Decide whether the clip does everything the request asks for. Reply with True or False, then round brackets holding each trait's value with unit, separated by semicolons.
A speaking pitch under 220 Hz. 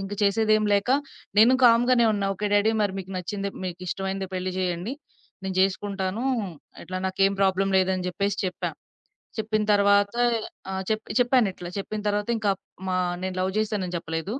True (200 Hz)